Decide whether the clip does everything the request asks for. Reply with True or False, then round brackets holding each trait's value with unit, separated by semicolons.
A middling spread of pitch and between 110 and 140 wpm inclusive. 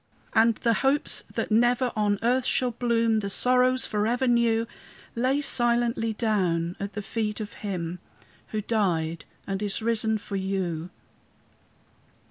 True (3.2 semitones; 135 wpm)